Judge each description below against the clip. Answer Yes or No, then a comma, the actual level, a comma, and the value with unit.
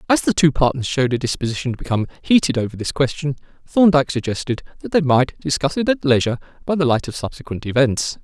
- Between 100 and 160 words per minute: No, fast, 205 wpm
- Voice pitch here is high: No, medium, 140 Hz